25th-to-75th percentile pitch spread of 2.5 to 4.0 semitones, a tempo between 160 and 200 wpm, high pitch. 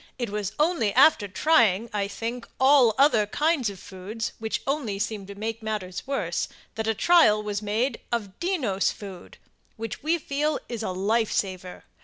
No: average, 5.0 semitones; average, 170 wpm; high, 220 Hz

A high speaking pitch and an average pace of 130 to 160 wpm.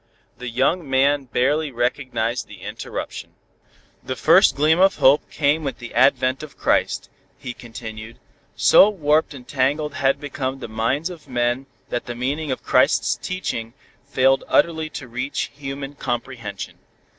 No: low, 135 Hz; average, 145 wpm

